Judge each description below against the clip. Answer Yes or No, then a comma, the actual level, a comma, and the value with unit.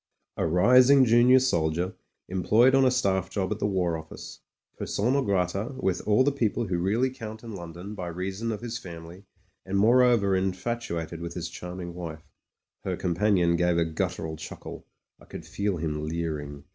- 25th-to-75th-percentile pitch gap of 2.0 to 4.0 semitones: No, average, 5.0 semitones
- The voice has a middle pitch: No, very low, 95 Hz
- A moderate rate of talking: Yes, average, 170 wpm